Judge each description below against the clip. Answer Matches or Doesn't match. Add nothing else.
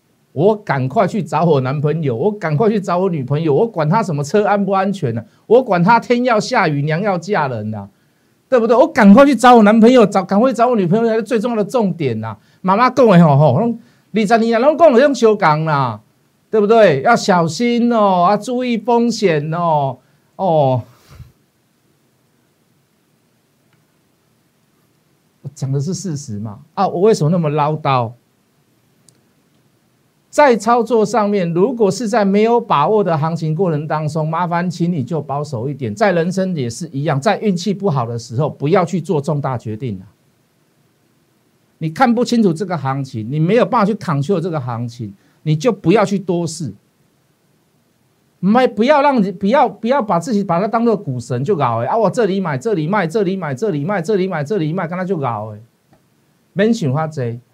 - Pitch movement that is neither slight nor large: Doesn't match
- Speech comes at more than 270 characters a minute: Doesn't match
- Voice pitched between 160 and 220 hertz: Matches